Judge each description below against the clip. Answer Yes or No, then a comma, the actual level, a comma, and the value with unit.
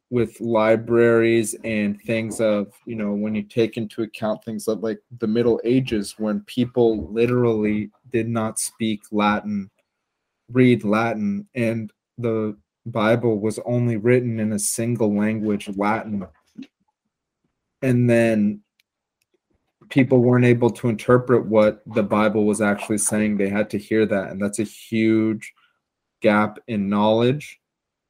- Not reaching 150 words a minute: Yes, slow, 135 wpm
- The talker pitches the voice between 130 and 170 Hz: No, low, 110 Hz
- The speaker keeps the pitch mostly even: Yes, narrow, 1.9 semitones